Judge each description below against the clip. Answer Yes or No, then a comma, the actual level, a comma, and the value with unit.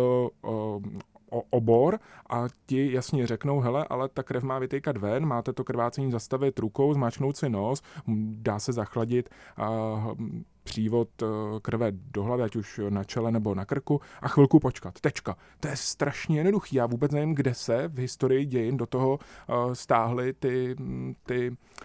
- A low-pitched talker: Yes, low, 125 Hz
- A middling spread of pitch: Yes, average, 3.1 semitones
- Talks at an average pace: Yes, average, 160 wpm